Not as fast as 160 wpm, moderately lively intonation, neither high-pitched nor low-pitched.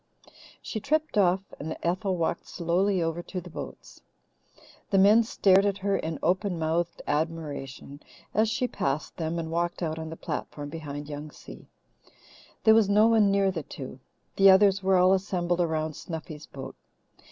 No: average, 165 wpm; average, 3.6 semitones; medium, 175 Hz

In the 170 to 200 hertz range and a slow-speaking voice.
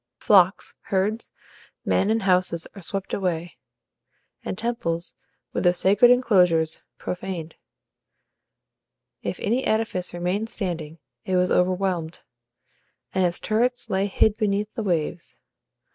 Yes: high, 190 Hz; slow, 115 wpm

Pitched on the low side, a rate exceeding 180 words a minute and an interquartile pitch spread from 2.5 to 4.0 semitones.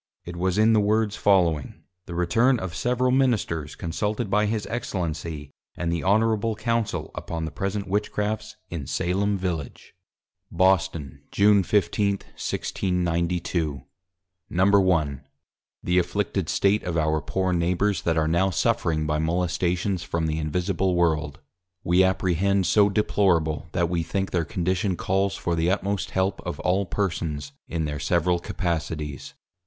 No: very low, 90 Hz; average, 140 wpm; average, 3.3 semitones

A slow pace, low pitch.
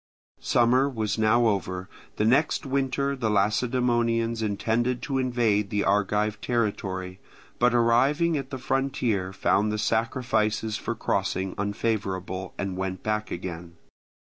Yes: slow, 125 wpm; low, 110 Hz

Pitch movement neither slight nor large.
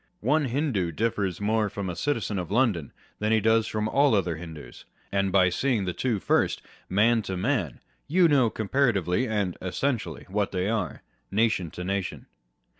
Yes: average, 4.0 semitones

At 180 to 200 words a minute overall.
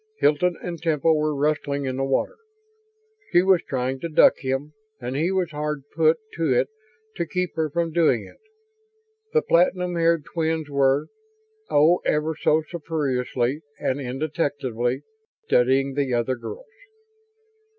No: average, 140 wpm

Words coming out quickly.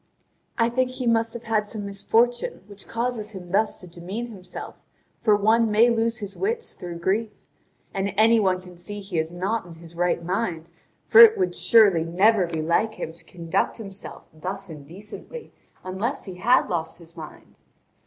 No: average, 185 wpm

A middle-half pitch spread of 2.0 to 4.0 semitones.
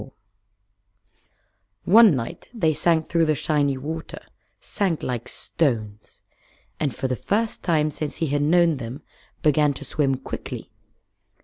Yes: average, 3.5 semitones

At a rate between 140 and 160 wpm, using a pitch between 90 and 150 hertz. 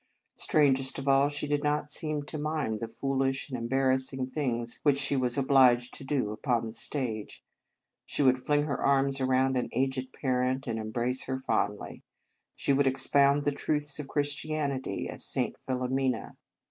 No: average, 170 wpm; low, 135 Hz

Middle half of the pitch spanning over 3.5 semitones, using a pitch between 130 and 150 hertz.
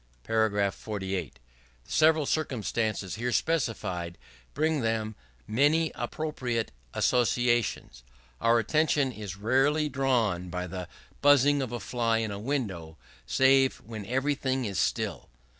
No: average, 5.1 semitones; low, 120 Hz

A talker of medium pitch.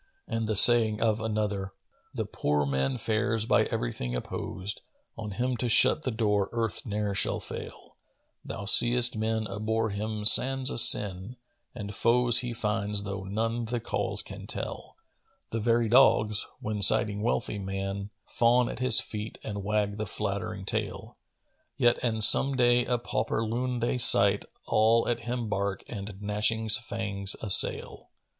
No: low, 110 Hz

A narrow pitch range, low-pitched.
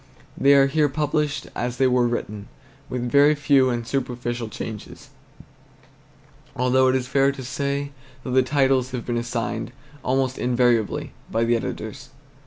Yes: narrow, 2.3 semitones; low, 130 Hz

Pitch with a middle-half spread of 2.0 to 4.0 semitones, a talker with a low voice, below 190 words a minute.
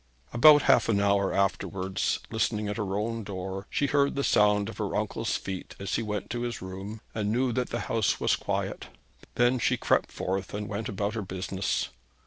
No: average, 2.7 semitones; low, 105 Hz; average, 195 wpm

